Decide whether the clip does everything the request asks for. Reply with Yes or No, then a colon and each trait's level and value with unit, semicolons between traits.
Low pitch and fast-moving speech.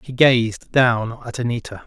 No: low, 120 Hz; average, 160 wpm